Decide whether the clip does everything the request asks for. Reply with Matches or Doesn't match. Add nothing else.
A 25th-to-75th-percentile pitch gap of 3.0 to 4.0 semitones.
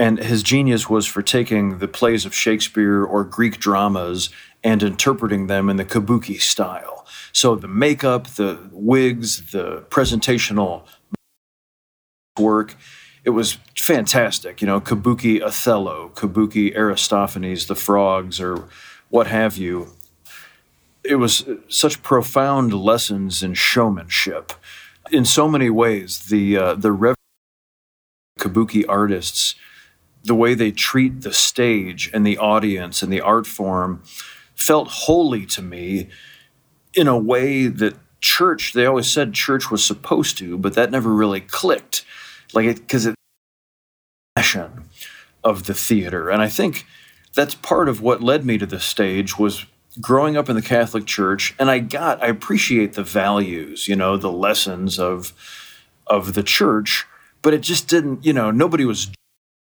Matches